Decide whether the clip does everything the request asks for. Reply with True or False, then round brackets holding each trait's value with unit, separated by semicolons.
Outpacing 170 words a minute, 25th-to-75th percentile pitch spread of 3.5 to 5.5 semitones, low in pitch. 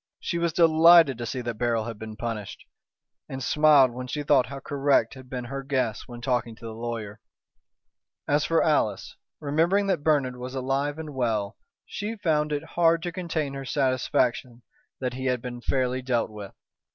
True (180 wpm; 4.0 semitones; 130 Hz)